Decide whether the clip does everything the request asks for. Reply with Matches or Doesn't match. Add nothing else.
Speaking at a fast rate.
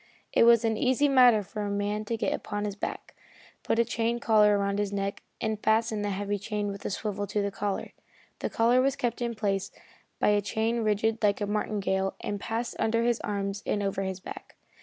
Matches